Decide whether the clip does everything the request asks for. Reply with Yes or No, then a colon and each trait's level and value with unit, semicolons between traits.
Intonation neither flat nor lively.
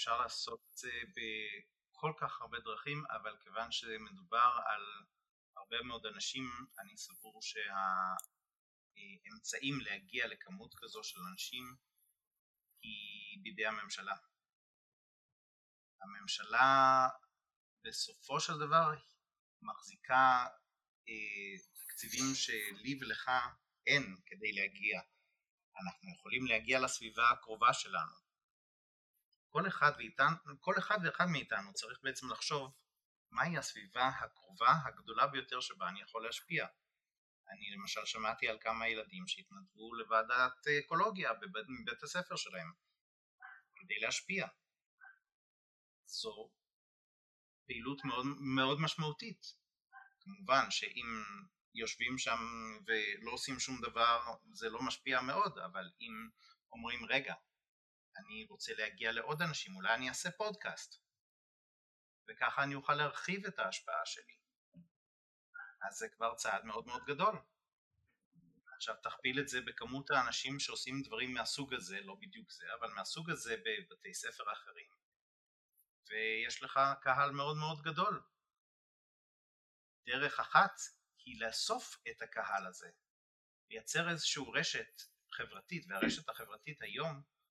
No: wide, 8.7 semitones